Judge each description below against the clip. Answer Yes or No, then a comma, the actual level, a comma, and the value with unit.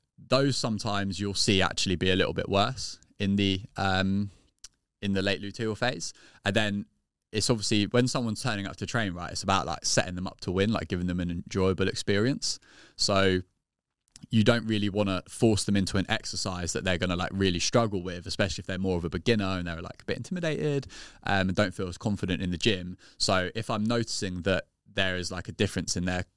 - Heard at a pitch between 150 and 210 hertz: No, low, 100 Hz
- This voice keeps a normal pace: No, fast, 220 wpm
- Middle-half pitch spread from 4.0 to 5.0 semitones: No, average, 2.8 semitones